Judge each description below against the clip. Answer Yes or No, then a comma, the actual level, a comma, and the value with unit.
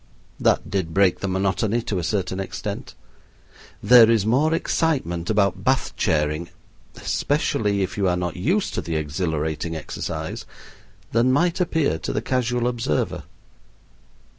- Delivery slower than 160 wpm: Yes, average, 140 wpm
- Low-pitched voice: Yes, low, 100 Hz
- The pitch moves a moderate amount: No, wide, 6.1 semitones